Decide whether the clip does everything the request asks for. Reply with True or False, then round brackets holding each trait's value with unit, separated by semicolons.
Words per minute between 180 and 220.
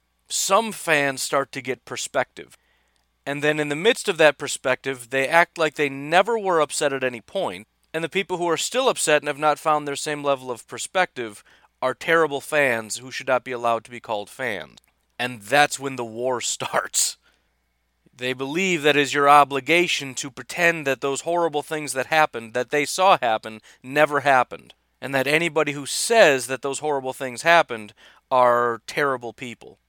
True (185 wpm)